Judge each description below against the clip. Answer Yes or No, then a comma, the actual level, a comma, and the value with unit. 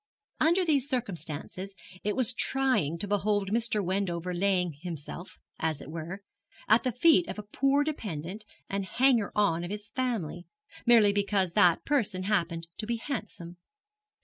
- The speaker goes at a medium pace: Yes, average, 155 wpm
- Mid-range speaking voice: No, high, 200 Hz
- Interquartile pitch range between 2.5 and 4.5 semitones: No, average, 5.3 semitones